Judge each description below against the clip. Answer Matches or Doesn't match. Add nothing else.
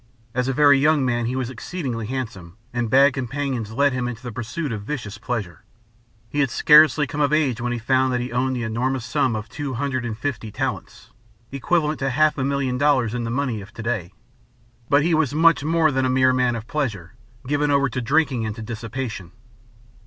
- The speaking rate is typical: Doesn't match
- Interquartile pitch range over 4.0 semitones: Doesn't match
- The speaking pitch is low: Matches